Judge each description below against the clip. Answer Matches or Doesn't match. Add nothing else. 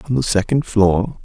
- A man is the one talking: Matches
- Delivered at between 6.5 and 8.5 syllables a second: Doesn't match